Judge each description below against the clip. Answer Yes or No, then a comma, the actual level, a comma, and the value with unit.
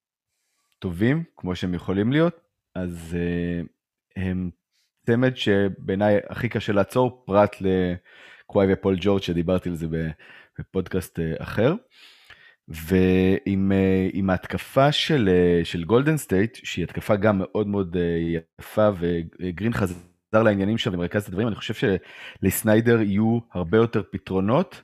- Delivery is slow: No, average, 120 wpm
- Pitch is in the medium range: No, very low, 95 Hz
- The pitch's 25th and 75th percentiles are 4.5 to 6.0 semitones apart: No, average, 3.3 semitones